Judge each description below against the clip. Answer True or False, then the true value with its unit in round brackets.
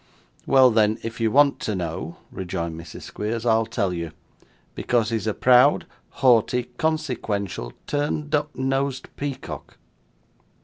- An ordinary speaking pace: False (130 wpm)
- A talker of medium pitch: False (115 Hz)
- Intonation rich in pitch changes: False (4.9 semitones)